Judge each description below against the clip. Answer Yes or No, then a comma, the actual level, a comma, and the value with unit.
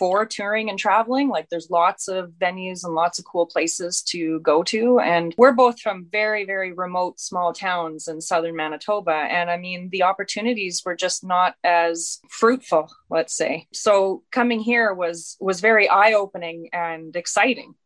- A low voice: No, medium, 180 Hz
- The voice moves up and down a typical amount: Yes, average, 3.7 semitones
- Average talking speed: Yes, average, 170 wpm